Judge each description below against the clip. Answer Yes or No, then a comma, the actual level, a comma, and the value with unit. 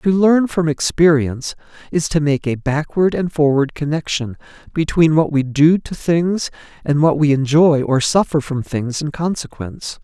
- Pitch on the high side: No, medium, 155 Hz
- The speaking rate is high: No, average, 165 wpm